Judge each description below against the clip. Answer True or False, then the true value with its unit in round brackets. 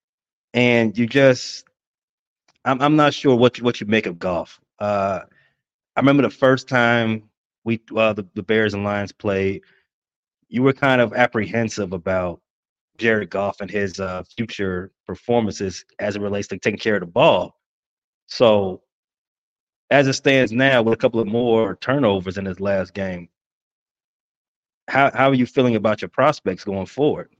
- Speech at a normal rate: True (165 wpm)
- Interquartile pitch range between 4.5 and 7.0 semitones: False (4.0 semitones)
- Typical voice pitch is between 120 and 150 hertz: False (110 Hz)